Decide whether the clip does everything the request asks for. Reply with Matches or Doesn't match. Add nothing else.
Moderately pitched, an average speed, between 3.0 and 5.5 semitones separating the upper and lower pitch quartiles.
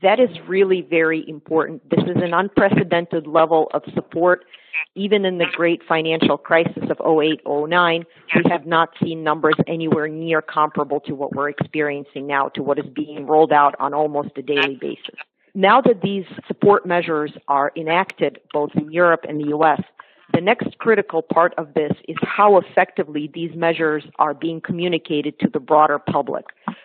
Doesn't match